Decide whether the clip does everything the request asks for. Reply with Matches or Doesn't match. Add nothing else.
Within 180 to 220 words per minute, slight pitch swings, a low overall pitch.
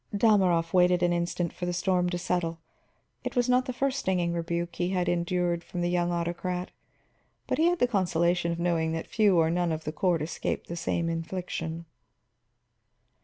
Doesn't match